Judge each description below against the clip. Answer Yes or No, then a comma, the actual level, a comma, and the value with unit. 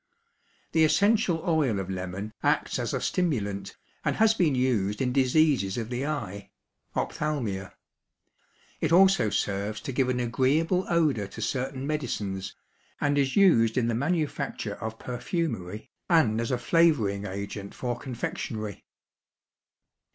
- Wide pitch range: Yes, wide, 6.7 semitones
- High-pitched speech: No, low, 125 Hz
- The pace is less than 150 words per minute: Yes, slow, 135 wpm